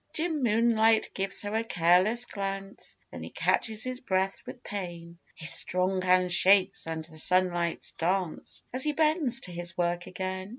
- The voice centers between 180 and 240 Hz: Yes, high, 190 Hz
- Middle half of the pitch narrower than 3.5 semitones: No, average, 4.3 semitones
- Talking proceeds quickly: No, average, 165 wpm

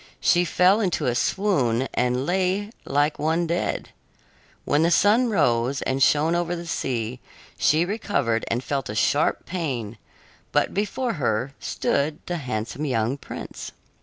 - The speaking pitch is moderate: Yes, medium, 150 Hz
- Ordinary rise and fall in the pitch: No, wide, 6.0 semitones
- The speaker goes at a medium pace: Yes, average, 145 wpm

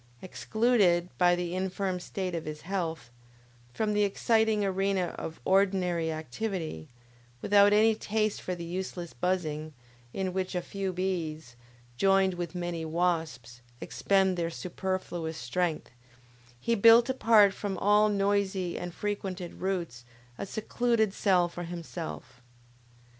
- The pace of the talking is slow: Yes, slow, 125 wpm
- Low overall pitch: No, medium, 185 Hz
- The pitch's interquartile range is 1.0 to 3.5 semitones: Yes, average, 2.9 semitones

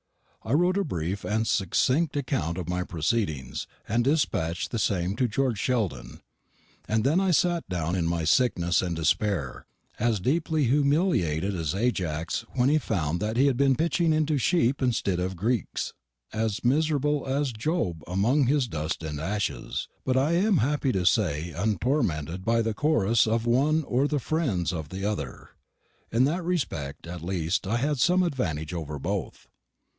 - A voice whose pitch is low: Yes, low, 115 Hz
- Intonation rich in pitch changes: Yes, wide, 8.3 semitones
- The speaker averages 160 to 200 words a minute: Yes, average, 165 wpm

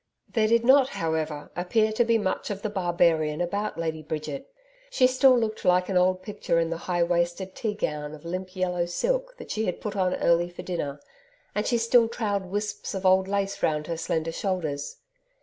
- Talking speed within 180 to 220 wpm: Yes, average, 200 wpm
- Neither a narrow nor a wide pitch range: Yes, average, 4.2 semitones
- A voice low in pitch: No, medium, 185 Hz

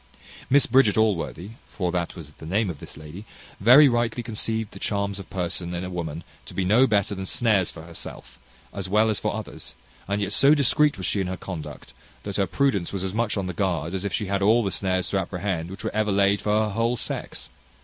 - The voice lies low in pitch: Yes, low, 100 Hz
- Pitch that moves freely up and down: No, average, 3.3 semitones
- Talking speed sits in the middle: No, fast, 230 wpm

